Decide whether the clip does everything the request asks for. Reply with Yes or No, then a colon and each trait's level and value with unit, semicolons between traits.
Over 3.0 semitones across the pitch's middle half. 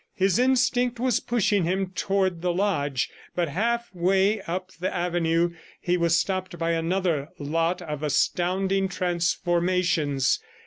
No: narrow, 2.6 semitones